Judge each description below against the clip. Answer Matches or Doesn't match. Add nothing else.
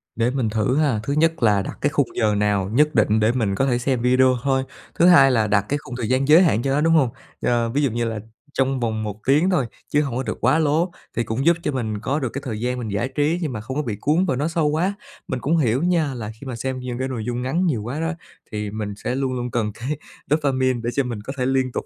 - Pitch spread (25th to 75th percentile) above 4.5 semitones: Doesn't match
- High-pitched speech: Doesn't match